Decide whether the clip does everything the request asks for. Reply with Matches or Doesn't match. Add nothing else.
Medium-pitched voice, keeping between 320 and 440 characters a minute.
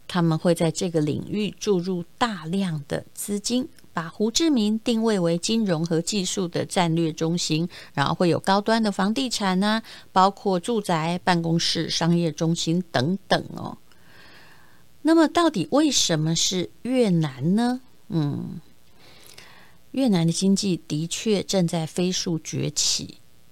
Doesn't match